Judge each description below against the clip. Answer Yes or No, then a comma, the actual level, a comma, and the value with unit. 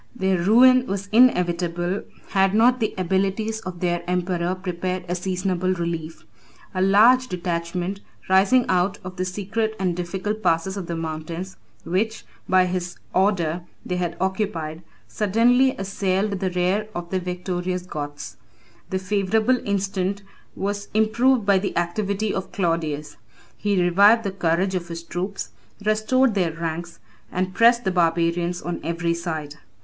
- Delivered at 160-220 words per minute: No, average, 145 wpm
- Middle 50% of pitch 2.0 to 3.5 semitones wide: Yes, average, 2.7 semitones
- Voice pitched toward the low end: No, medium, 185 Hz